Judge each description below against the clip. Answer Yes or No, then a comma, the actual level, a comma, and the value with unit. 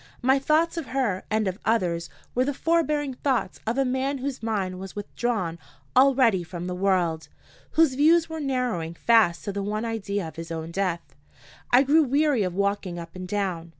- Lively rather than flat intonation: Yes, wide, 6.8 semitones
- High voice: Yes, high, 215 Hz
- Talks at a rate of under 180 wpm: No, average, 185 wpm